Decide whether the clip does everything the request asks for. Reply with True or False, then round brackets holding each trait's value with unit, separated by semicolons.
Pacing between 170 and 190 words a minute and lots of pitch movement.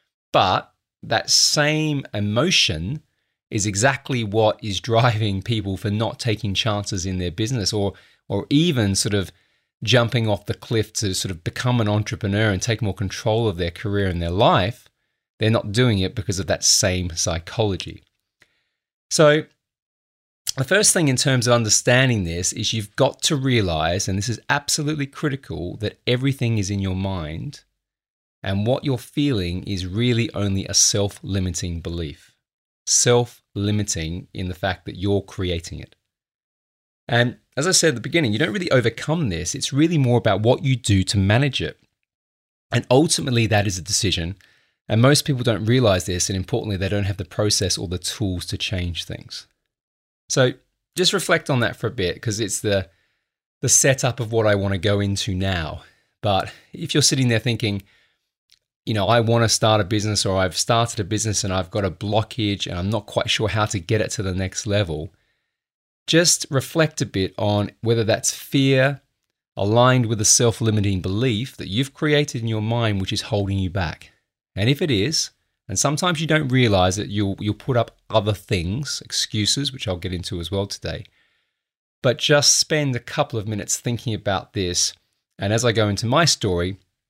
False (185 wpm; 4.3 semitones)